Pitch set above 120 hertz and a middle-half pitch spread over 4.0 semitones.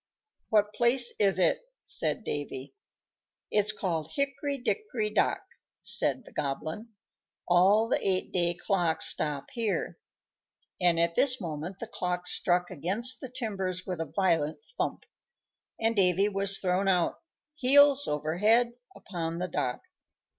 Yes: high, 190 Hz; average, 5.0 semitones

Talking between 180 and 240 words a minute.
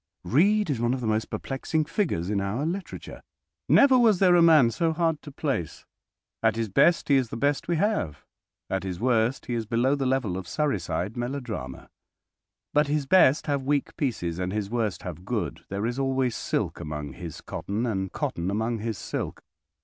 Yes: average, 190 wpm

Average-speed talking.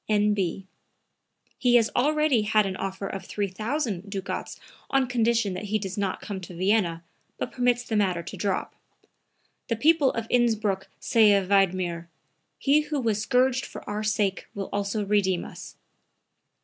Yes: average, 155 wpm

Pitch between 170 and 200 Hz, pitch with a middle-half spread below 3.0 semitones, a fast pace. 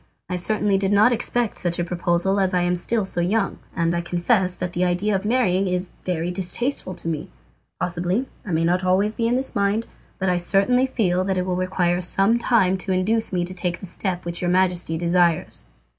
Yes: medium, 185 Hz; narrow, 2.5 semitones; fast, 215 wpm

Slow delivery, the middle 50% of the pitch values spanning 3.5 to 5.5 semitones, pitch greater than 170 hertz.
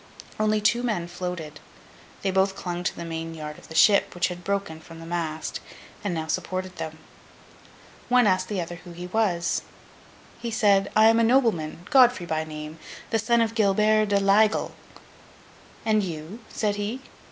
No: average, 175 wpm; average, 4.3 semitones; high, 190 Hz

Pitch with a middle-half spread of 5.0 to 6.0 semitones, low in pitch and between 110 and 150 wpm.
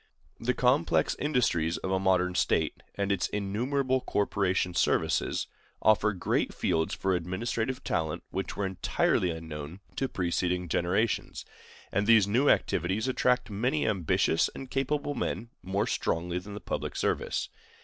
Yes: wide, 5.4 semitones; low, 100 Hz; average, 140 wpm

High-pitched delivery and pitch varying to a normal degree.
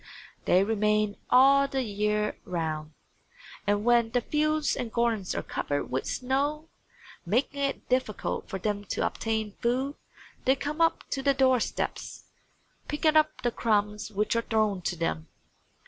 Yes: high, 230 Hz; average, 4.8 semitones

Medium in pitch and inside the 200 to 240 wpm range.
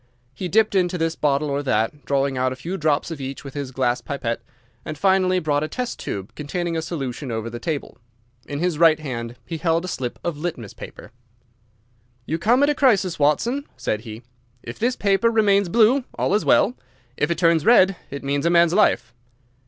Yes: medium, 160 Hz; fast, 205 wpm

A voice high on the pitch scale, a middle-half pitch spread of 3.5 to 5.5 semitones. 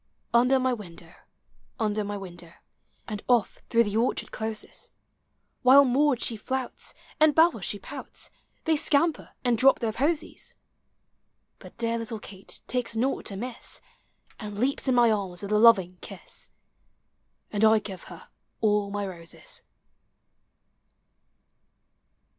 Yes: high, 225 Hz; average, 3.8 semitones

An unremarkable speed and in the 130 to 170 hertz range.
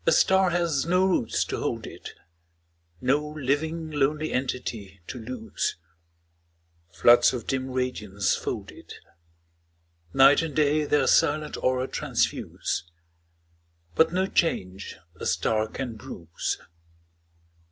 No: slow, 115 wpm; low, 135 Hz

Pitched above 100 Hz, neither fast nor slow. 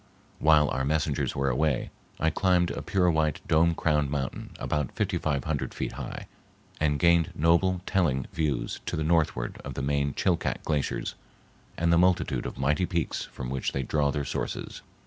No: very low, 75 Hz; average, 175 wpm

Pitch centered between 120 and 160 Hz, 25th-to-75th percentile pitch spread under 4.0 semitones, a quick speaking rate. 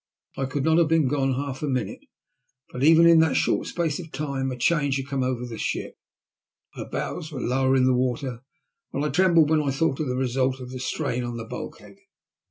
Yes: low, 135 Hz; average, 3.2 semitones; fast, 220 wpm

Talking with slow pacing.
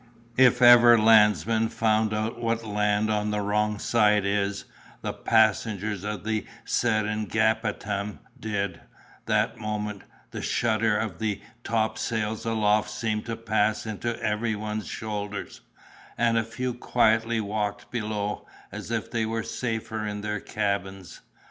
Yes: slow, 130 wpm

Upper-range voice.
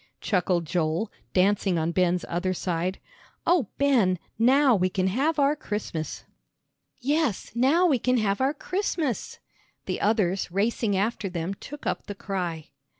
Yes: high, 200 Hz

